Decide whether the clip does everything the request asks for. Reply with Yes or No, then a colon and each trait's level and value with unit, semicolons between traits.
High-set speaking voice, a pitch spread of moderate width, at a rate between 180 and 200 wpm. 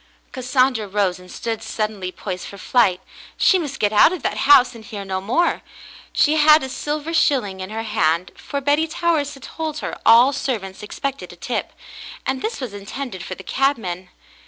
No: high, 235 Hz; wide, 6.4 semitones; average, 185 wpm